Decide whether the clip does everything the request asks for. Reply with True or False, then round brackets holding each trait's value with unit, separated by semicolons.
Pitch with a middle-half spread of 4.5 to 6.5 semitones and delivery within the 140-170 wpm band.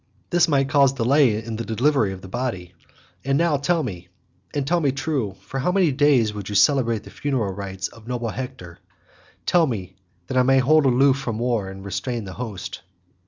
False (5.0 semitones; 200 wpm)